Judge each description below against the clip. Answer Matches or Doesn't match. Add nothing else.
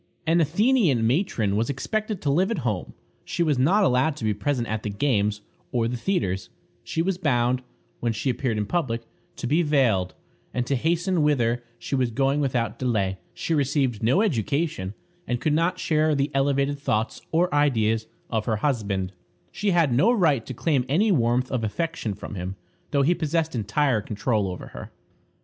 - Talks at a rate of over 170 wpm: Matches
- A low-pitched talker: Matches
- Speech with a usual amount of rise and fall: Doesn't match